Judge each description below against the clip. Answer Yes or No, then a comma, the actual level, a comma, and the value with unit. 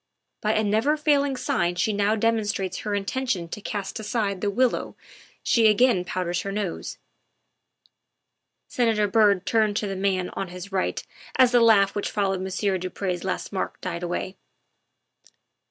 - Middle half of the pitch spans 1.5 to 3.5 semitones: Yes, average, 2.9 semitones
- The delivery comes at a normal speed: Yes, average, 155 wpm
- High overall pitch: Yes, high, 205 Hz